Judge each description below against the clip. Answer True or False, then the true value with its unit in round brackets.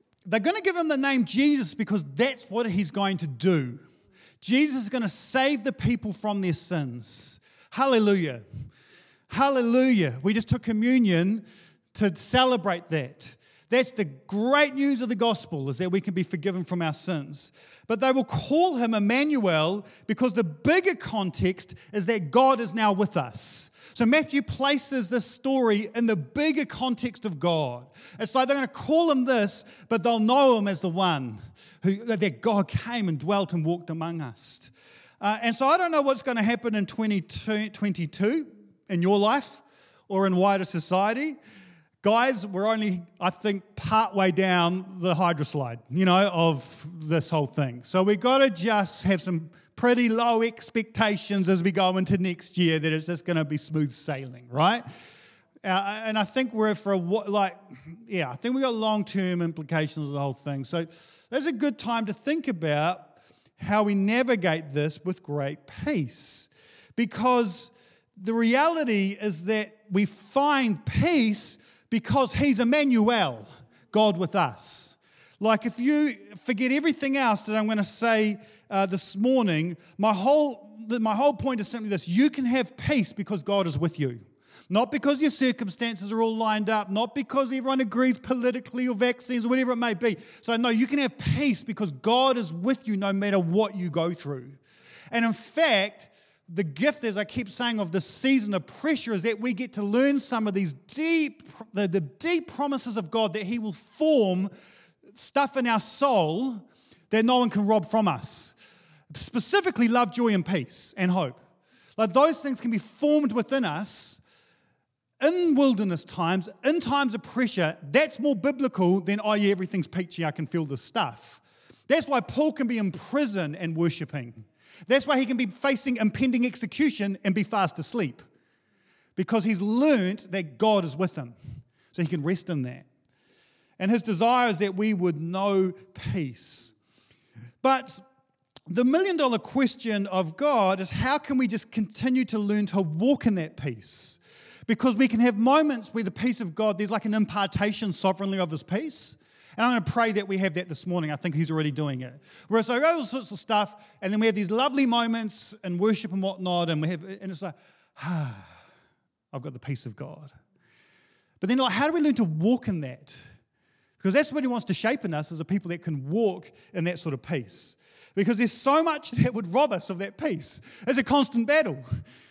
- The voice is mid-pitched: False (210 Hz)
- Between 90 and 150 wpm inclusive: False (185 wpm)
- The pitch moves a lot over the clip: True (5.9 semitones)